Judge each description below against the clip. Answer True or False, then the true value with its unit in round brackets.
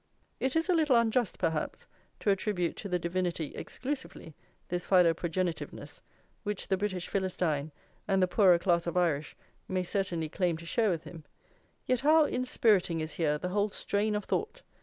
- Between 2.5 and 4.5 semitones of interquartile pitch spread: True (3.9 semitones)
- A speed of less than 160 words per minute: False (165 wpm)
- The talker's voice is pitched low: False (185 Hz)